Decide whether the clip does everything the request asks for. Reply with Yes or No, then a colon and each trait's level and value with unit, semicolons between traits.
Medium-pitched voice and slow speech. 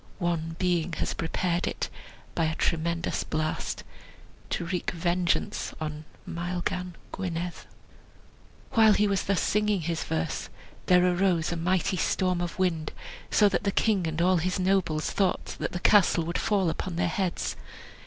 No: medium, 175 Hz; average, 155 wpm